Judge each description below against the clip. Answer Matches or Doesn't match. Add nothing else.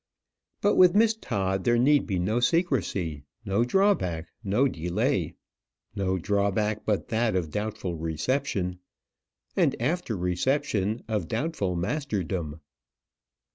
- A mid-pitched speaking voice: Doesn't match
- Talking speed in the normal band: Doesn't match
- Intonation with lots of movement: Matches